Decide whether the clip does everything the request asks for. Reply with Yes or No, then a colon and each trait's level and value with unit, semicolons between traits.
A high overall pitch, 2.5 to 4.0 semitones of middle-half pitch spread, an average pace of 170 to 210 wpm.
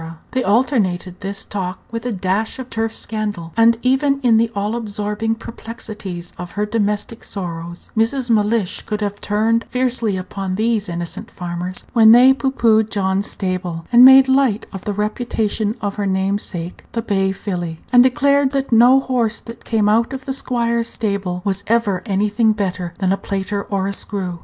Yes: high, 210 Hz; average, 3.3 semitones; average, 175 wpm